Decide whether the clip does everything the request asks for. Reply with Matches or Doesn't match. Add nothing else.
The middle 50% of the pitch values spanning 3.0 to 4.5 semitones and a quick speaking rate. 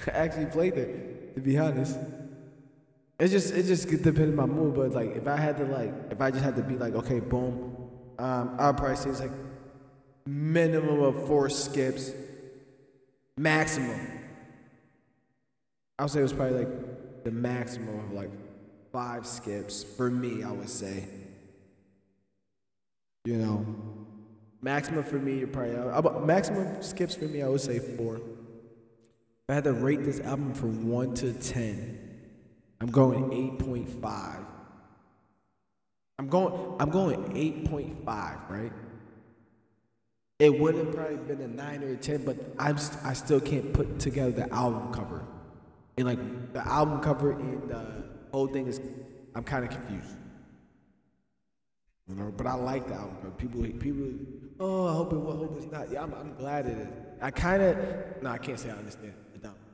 Doesn't match